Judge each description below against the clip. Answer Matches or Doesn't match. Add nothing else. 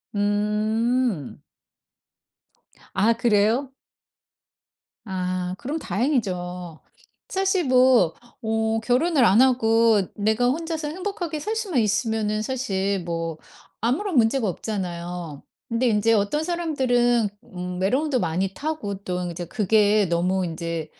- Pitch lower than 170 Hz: Doesn't match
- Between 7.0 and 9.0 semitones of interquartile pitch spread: Doesn't match